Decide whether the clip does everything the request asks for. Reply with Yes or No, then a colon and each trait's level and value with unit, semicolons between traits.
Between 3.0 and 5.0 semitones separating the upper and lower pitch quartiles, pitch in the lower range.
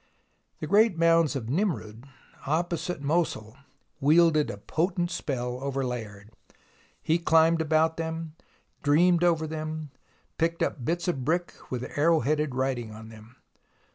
No: average, 4.5 semitones; medium, 155 Hz